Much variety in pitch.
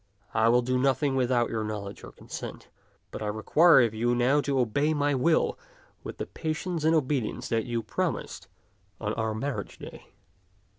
No: average, 4.3 semitones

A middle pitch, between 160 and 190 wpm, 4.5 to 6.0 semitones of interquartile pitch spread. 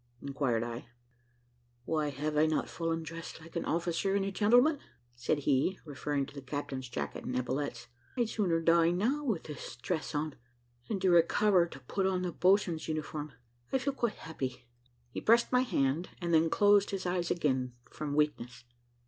Yes: medium, 165 Hz; average, 175 wpm; average, 5.1 semitones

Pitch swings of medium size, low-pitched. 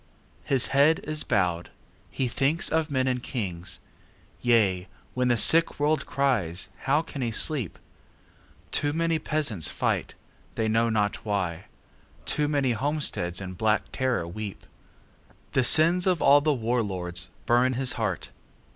No: wide, 6.1 semitones; low, 125 Hz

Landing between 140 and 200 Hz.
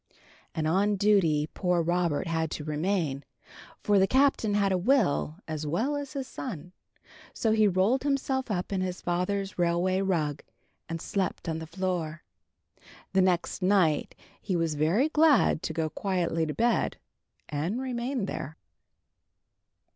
Yes: medium, 185 Hz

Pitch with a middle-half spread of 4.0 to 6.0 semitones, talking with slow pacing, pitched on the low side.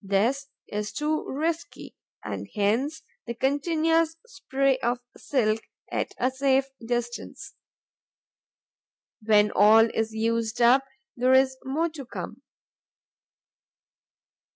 No: average, 4.3 semitones; slow, 105 wpm; very high, 260 Hz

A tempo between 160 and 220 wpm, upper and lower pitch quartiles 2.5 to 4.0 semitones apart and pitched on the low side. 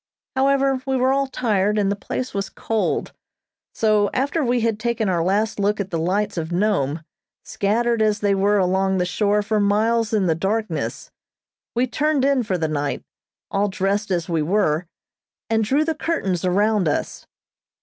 No: average, 175 wpm; average, 3.7 semitones; high, 210 Hz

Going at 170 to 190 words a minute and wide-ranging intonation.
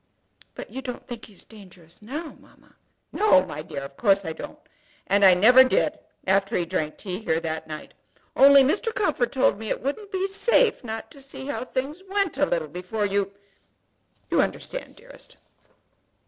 Yes: average, 180 wpm; wide, 7.5 semitones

